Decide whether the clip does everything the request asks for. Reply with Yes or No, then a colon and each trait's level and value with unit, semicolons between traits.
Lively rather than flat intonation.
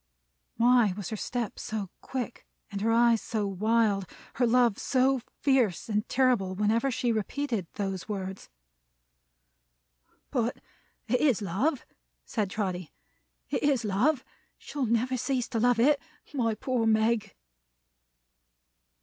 No: average, 3.4 semitones